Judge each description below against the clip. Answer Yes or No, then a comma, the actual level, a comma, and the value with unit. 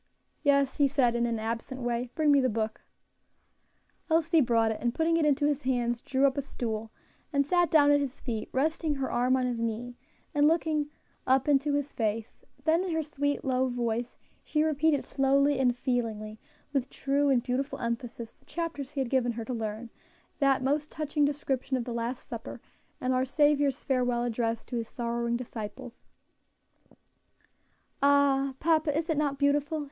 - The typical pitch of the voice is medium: No, very high, 265 Hz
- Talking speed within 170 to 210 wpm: Yes, average, 180 wpm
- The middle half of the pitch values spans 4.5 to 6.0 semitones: No, average, 3.4 semitones